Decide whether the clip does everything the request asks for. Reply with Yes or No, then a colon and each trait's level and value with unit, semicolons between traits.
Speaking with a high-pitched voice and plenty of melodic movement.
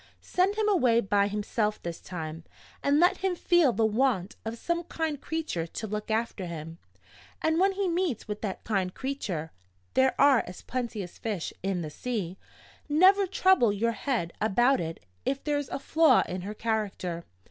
Yes: high, 225 Hz; wide, 7.6 semitones